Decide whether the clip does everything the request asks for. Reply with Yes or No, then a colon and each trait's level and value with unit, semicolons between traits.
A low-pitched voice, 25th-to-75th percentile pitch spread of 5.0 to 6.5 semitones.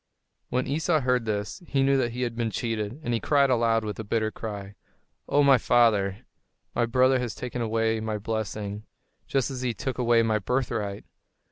No: low, 115 Hz; average, 2.7 semitones